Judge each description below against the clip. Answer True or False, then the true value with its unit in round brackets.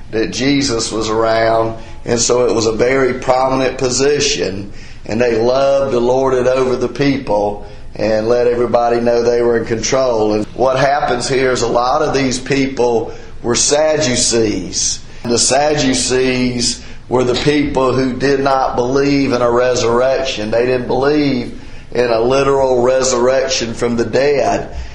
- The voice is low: True (125 Hz)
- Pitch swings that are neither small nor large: False (2.2 semitones)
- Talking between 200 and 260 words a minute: False (155 wpm)